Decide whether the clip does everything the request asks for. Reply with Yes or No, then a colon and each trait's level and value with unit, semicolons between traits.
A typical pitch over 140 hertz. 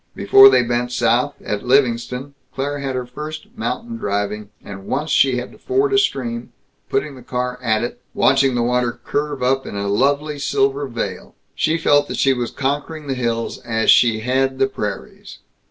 No: low, 125 Hz